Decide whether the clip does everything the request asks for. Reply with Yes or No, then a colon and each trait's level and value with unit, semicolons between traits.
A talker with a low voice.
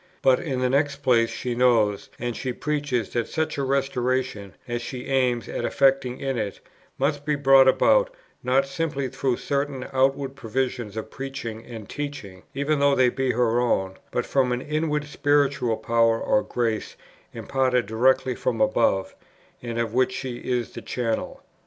Yes: low, 130 Hz